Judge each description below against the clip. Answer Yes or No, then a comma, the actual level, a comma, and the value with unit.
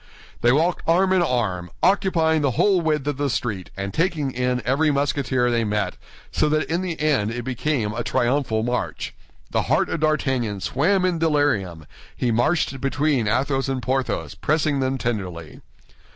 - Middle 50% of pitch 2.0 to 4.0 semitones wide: No, average, 4.5 semitones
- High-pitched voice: No, low, 135 Hz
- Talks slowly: No, average, 165 wpm